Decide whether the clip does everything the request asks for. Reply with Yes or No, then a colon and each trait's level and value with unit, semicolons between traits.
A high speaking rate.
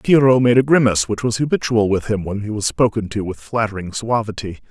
Yes: fast, 215 wpm